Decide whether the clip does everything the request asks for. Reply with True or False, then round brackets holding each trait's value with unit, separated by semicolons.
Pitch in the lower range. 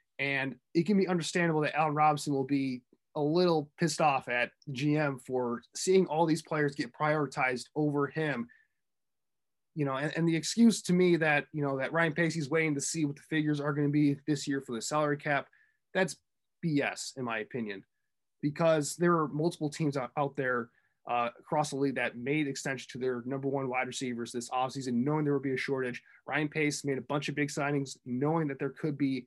False (145 Hz)